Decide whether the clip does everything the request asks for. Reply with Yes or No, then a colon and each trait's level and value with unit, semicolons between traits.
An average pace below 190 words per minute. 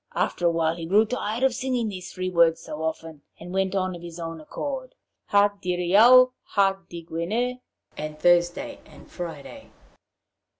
Yes: average, 160 wpm